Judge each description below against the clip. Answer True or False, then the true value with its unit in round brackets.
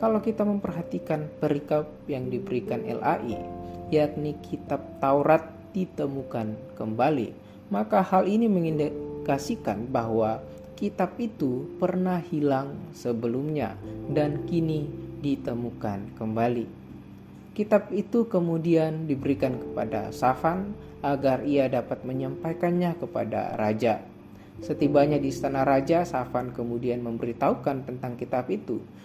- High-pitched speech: False (140 Hz)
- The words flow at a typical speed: True (100 wpm)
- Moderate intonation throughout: False (5.7 semitones)